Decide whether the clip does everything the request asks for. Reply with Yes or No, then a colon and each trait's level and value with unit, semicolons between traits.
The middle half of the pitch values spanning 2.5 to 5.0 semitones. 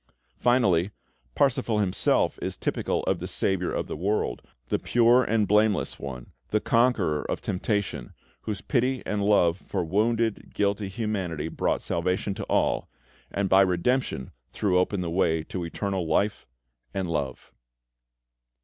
Yes: average, 3.7 semitones